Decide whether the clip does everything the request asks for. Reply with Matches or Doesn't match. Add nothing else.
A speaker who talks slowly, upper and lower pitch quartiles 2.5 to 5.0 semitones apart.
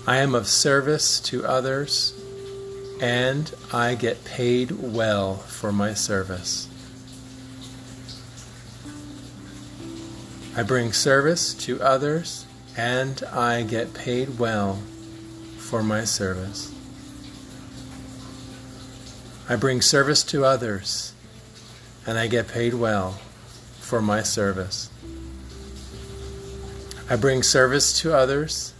Matches